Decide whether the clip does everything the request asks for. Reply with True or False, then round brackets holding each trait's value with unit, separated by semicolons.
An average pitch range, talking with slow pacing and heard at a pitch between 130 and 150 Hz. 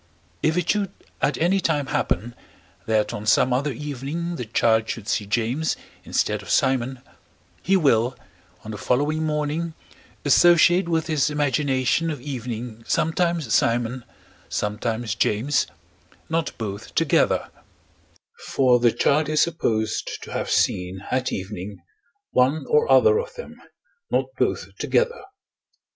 False (5.8 semitones; 130 wpm; 135 Hz)